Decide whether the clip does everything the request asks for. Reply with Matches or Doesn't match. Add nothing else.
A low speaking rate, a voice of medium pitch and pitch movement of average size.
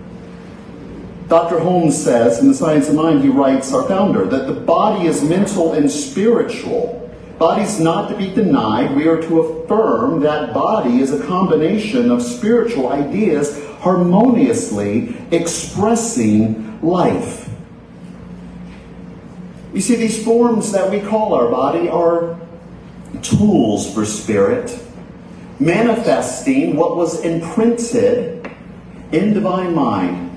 Doesn't match